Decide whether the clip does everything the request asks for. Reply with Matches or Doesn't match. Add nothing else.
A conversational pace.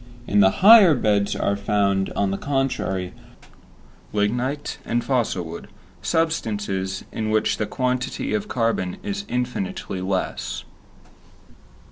Doesn't match